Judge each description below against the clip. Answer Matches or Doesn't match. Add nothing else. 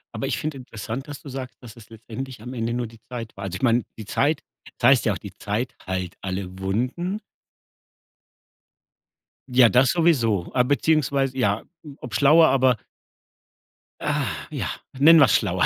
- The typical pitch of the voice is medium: Doesn't match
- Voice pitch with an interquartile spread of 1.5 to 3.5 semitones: Doesn't match